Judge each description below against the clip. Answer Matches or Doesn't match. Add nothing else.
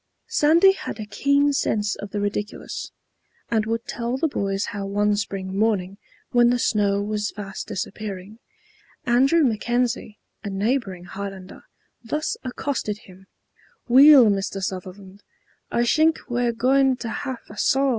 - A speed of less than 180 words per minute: Matches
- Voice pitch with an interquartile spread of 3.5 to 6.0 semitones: Matches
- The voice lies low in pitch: Doesn't match